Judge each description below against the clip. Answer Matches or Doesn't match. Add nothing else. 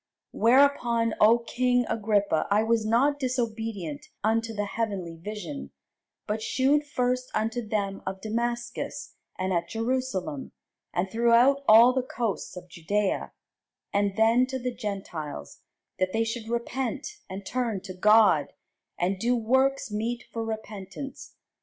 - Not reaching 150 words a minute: Matches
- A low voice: Doesn't match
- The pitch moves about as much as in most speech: Matches